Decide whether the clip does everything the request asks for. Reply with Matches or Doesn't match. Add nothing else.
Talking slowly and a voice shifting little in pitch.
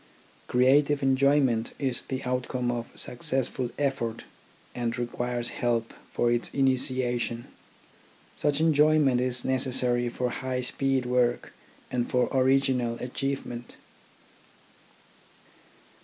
Matches